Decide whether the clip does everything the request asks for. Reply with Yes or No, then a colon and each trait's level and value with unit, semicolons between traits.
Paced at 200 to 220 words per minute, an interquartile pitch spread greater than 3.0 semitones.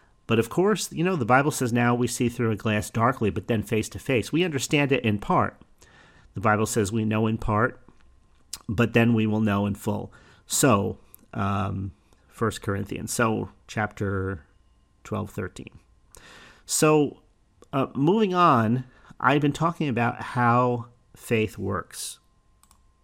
No: average, 150 wpm; average, 3.6 semitones